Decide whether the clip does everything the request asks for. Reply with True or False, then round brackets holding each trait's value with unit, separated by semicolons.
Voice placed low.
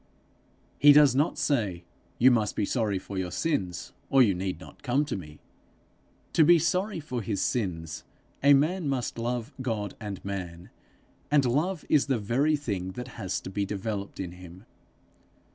True (115 Hz)